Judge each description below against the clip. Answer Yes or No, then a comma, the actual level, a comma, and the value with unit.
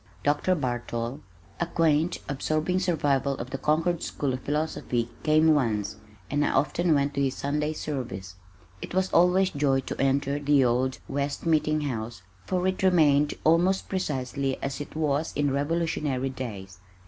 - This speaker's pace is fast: No, average, 155 wpm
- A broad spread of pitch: No, average, 3.2 semitones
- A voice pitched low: No, medium, 145 Hz